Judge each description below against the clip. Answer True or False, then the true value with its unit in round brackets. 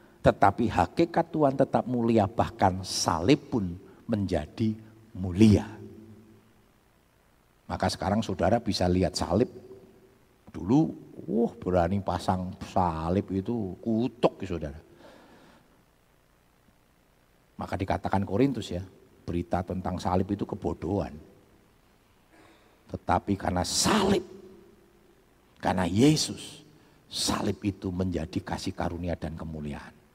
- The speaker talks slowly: False (95 wpm)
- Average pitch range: True (3.9 semitones)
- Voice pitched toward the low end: True (100 Hz)